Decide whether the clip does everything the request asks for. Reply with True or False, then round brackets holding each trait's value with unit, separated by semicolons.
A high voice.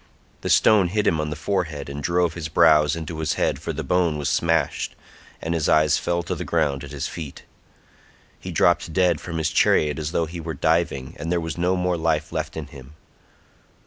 False (80 Hz)